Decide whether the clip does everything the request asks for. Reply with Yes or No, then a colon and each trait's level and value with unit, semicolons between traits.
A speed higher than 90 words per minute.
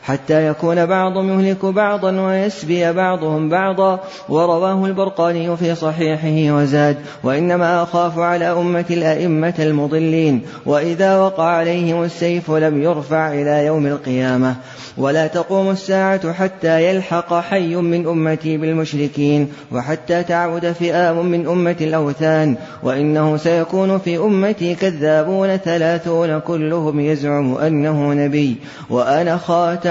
Yes: average, 110 wpm